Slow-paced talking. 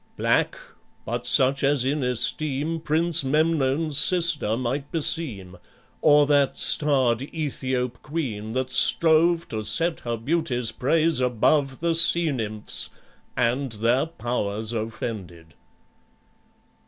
Yes: slow, 110 wpm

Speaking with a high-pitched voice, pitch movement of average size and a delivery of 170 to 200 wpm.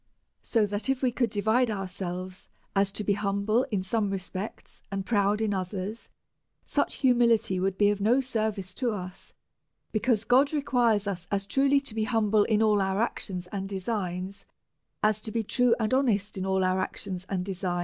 Yes: high, 210 Hz; average, 3.0 semitones; average, 175 wpm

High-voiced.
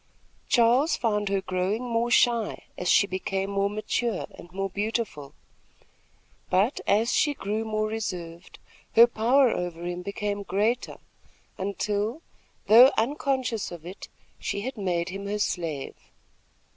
Yes: high, 205 Hz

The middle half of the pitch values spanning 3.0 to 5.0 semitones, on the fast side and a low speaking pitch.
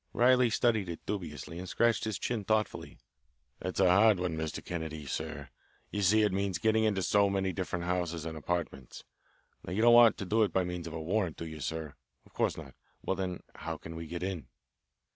Yes: average, 4.3 semitones; fast, 210 wpm; very low, 90 Hz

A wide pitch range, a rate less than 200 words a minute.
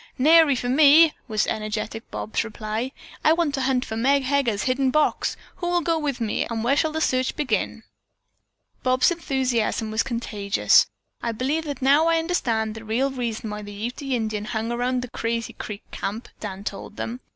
No: average, 4.3 semitones; average, 185 wpm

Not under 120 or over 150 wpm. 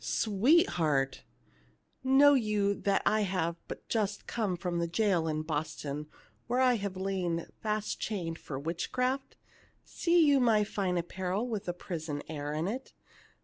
No: average, 160 wpm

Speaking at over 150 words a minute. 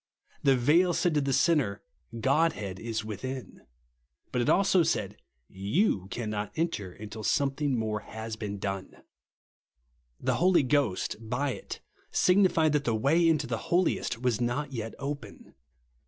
No: average, 145 wpm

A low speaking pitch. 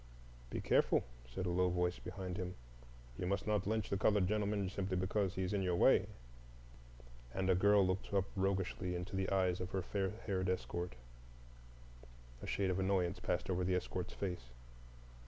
Yes: very low, 95 Hz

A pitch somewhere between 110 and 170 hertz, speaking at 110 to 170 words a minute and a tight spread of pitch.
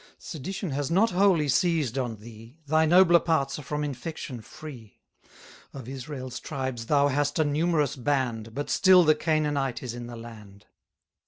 No: medium, 140 Hz; average, 160 wpm; average, 4.4 semitones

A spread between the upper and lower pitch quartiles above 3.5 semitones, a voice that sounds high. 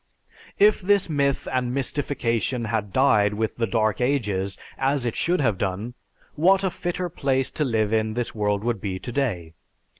No: average, 4.9 semitones; low, 120 Hz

